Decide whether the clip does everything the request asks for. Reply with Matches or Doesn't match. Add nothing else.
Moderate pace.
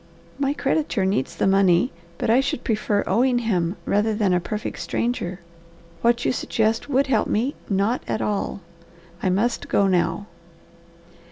Matches